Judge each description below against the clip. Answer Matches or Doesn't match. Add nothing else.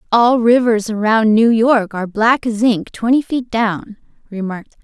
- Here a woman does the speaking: Matches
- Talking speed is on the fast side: Doesn't match